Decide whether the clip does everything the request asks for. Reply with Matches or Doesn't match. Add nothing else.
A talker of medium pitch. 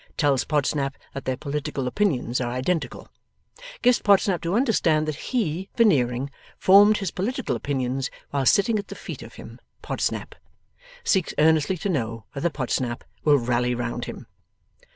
Matches